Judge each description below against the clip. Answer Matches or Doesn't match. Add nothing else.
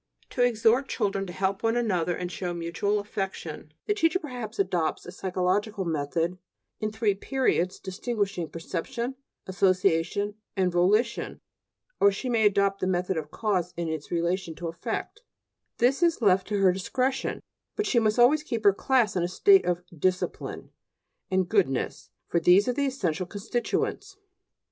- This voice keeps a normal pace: Matches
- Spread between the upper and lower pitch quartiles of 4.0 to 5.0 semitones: Matches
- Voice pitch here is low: Doesn't match